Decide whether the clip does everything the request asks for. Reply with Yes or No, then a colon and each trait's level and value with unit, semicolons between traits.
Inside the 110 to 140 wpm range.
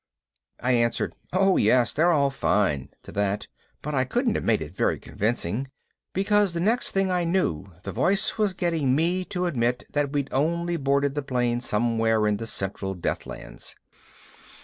No: average, 170 wpm